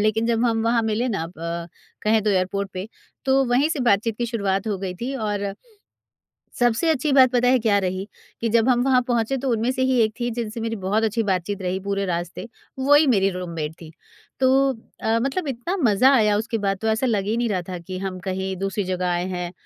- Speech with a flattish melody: No, average, 4.0 semitones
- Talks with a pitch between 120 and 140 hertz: No, high, 220 Hz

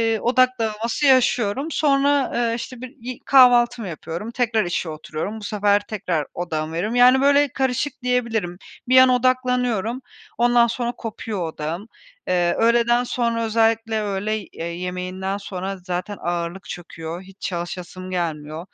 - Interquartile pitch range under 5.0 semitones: No, average, 5.3 semitones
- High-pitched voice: Yes, high, 220 Hz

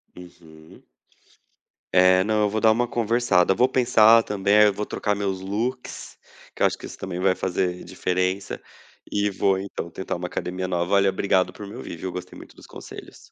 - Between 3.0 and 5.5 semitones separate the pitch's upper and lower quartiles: No, narrow, 2.5 semitones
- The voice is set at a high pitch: No, very low, 95 Hz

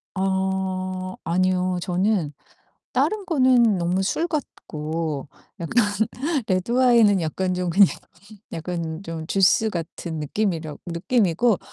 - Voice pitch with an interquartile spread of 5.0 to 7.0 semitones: No, average, 3.6 semitones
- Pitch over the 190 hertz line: No, medium, 185 Hz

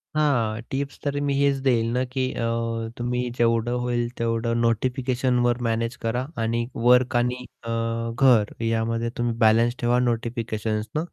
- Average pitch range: No, narrow, 1.5 semitones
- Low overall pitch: Yes, low, 120 Hz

